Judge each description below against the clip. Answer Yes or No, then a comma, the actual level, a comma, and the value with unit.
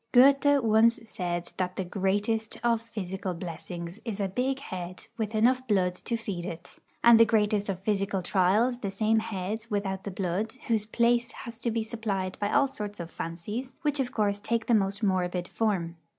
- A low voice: No, high, 210 Hz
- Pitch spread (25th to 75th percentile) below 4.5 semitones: Yes, average, 3.6 semitones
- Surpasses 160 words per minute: Yes, average, 185 wpm